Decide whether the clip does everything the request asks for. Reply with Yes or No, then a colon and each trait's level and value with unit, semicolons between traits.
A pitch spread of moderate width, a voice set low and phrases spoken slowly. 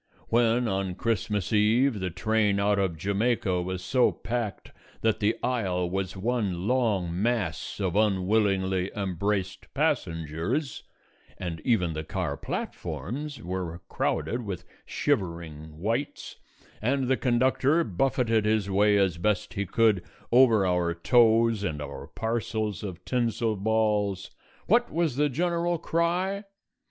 Yes: average, 4.4 semitones; low, 105 Hz; slow, 125 wpm